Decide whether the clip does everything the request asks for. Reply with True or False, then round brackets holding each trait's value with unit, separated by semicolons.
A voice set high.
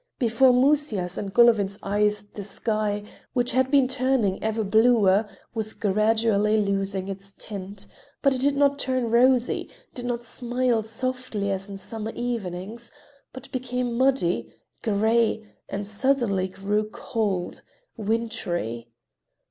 True (220 Hz)